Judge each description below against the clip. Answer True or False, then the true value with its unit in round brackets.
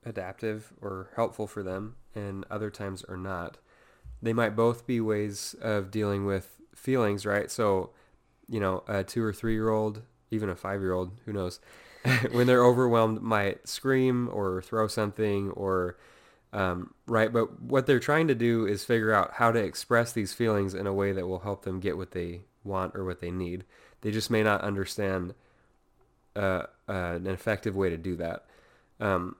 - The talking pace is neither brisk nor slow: True (185 wpm)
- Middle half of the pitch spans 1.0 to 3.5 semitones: True (3.1 semitones)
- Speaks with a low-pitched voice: True (105 Hz)